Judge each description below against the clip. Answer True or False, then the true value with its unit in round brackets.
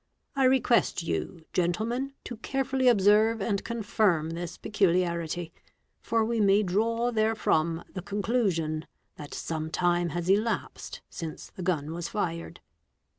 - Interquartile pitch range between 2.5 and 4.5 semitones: False (5.1 semitones)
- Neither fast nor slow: False (125 wpm)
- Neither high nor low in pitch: False (195 Hz)